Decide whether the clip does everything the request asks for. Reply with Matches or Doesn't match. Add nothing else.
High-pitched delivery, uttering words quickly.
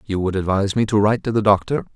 Doesn't match